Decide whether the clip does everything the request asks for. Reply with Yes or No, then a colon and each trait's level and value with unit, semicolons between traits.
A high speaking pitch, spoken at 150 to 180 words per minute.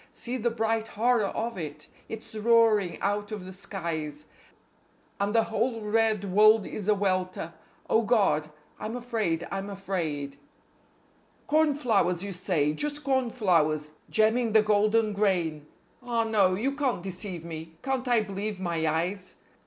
No: high, 205 Hz; average, 140 wpm